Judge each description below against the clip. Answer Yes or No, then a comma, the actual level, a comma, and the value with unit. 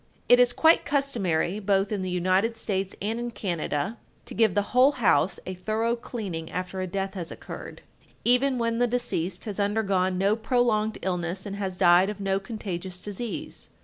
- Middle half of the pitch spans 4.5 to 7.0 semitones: No, average, 3.8 semitones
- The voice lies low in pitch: No, high, 200 Hz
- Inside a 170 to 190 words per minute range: Yes, average, 180 wpm